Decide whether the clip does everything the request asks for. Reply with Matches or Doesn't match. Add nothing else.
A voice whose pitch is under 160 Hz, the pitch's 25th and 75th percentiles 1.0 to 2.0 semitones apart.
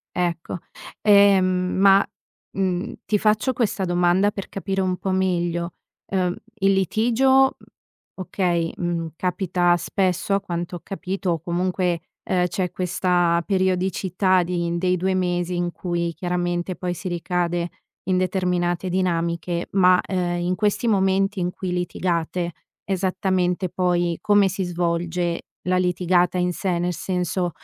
Doesn't match